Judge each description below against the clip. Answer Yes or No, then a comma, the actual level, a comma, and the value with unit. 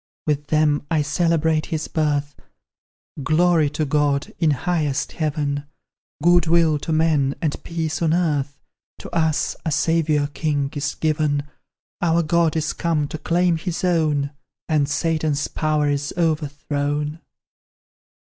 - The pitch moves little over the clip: Yes, narrow, 2.0 semitones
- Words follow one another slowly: Yes, slow, 130 wpm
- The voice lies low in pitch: No, medium, 155 Hz